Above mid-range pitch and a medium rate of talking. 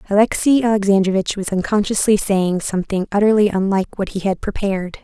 Yes: high, 200 Hz; average, 145 wpm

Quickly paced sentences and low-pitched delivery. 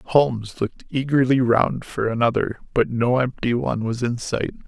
No: average, 165 wpm; low, 120 Hz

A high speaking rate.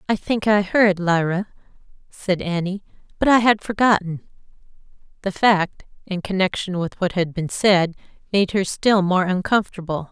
No: average, 150 wpm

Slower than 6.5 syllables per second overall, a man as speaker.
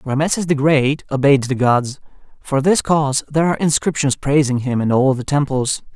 Yes: 5.3 syllables/s; male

